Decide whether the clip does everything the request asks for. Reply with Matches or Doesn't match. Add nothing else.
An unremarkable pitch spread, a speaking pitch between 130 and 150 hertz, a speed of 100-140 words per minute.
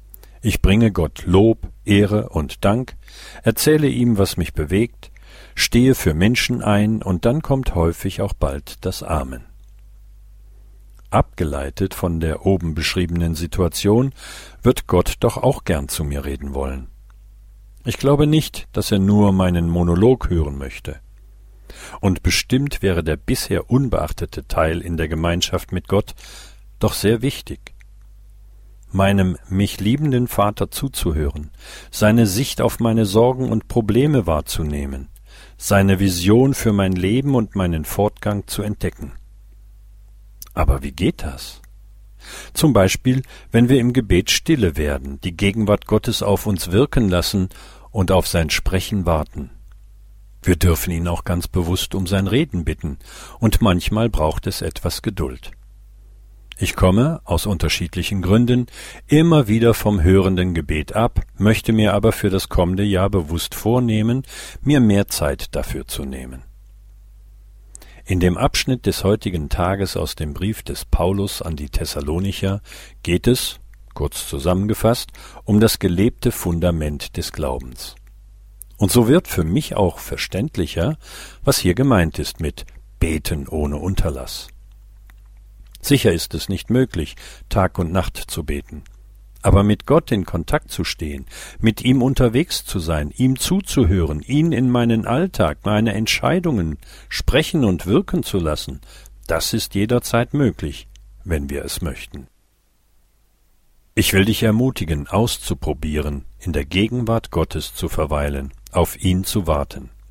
Doesn't match